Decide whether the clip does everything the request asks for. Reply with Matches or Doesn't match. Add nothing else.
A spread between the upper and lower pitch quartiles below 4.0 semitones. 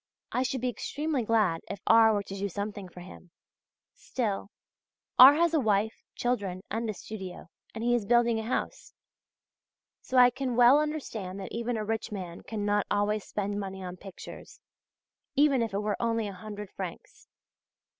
Matches